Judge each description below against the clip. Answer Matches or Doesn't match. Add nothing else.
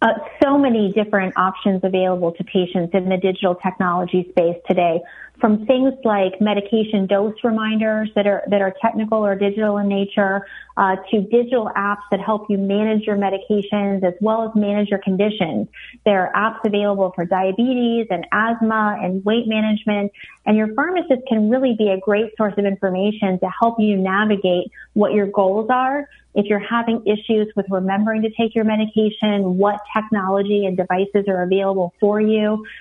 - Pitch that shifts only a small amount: Matches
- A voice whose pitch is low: Doesn't match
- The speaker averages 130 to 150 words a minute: Doesn't match